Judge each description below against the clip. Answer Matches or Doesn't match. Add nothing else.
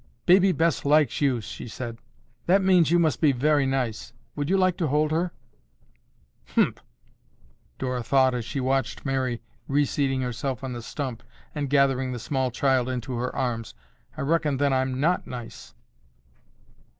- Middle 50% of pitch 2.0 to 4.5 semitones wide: Matches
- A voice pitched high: Doesn't match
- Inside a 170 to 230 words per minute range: Doesn't match